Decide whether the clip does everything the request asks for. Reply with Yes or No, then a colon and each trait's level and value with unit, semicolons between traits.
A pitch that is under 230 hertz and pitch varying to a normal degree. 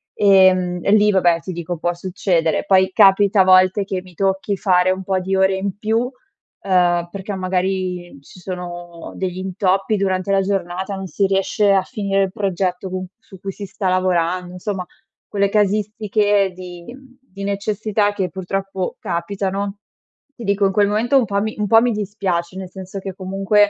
No: high, 190 Hz; narrow, 1.7 semitones